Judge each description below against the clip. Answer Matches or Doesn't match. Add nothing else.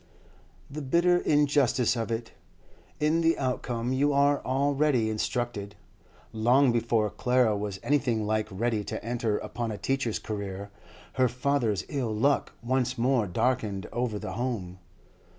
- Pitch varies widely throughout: Doesn't match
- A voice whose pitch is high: Doesn't match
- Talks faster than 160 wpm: Doesn't match